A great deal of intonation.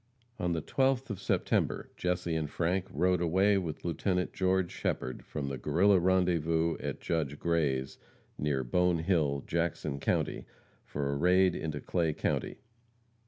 No: average, 3.6 semitones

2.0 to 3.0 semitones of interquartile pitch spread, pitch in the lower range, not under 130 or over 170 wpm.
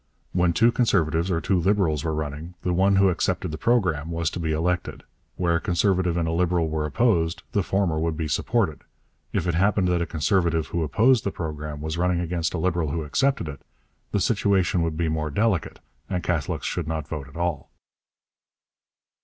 No: average, 2.7 semitones; very low, 85 Hz; average, 195 wpm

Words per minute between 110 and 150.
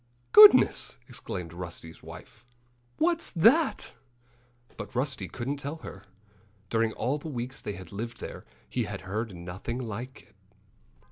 Yes: slow, 135 wpm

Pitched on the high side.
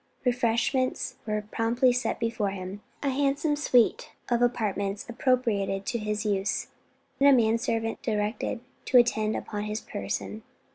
Yes: high, 225 Hz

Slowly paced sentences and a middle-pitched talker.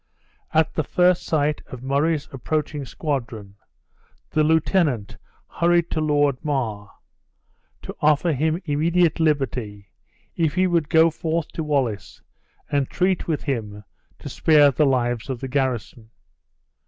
Yes: slow, 130 wpm; medium, 145 Hz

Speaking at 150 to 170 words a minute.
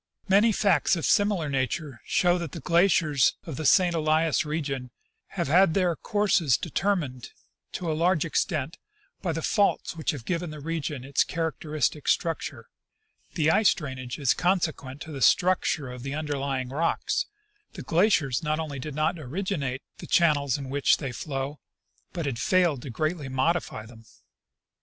Yes: average, 160 wpm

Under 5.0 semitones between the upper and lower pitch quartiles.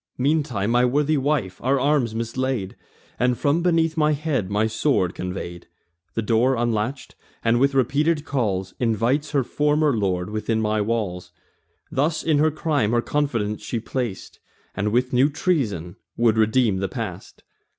No: average, 5.3 semitones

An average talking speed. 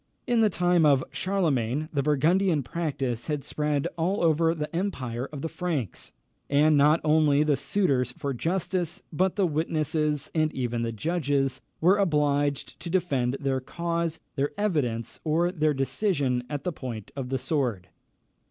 Yes: average, 150 wpm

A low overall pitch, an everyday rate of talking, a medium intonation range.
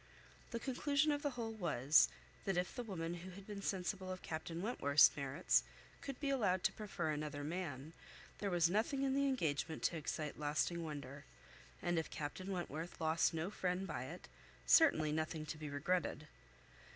No: medium, 175 Hz; average, 175 wpm; average, 5.0 semitones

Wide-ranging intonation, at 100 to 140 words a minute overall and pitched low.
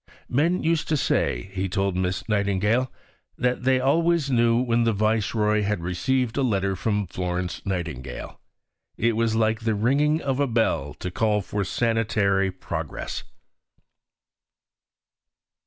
No: average, 4.4 semitones; slow, 135 wpm; low, 110 Hz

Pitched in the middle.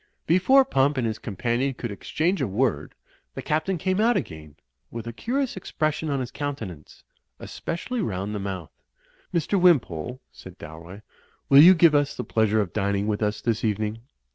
No: low, 120 Hz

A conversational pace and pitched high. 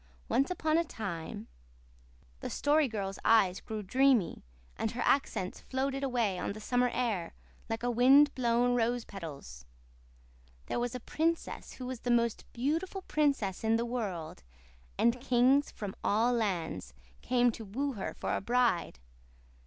Yes: average, 150 wpm; high, 240 Hz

